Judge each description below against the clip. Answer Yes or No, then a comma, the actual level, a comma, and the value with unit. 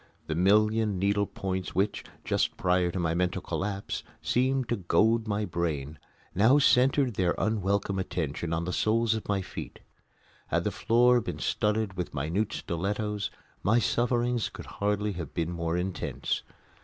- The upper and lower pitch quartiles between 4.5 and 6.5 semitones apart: No, average, 3.8 semitones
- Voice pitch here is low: Yes, low, 100 Hz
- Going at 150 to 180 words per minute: Yes, average, 155 wpm